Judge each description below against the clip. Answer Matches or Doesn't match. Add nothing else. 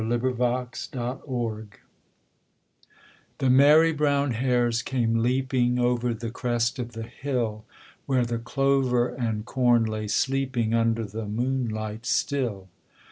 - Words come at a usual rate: Doesn't match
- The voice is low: Matches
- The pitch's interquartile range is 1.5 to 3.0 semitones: Matches